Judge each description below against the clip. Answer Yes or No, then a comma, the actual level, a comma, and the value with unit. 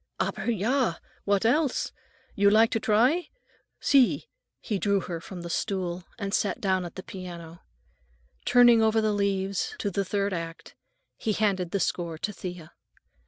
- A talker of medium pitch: No, high, 200 Hz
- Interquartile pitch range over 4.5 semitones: No, average, 3.5 semitones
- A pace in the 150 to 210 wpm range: Yes, average, 160 wpm